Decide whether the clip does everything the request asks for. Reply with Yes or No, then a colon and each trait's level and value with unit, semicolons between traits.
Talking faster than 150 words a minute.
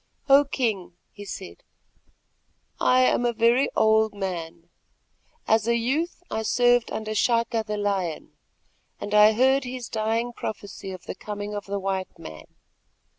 No: average, 145 wpm